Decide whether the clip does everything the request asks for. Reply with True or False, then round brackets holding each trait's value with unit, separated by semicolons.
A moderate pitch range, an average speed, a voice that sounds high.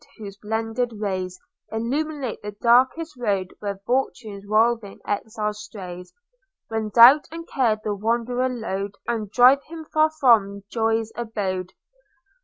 False (3.4 semitones; 125 wpm; 225 Hz)